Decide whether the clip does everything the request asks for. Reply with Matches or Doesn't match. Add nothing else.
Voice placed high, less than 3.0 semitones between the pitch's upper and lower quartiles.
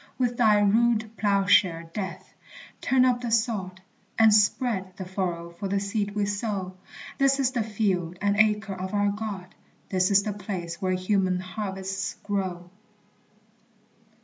Matches